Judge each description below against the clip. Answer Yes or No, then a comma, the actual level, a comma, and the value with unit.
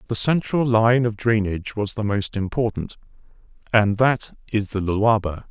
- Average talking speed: Yes, average, 155 wpm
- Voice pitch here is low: Yes, low, 110 Hz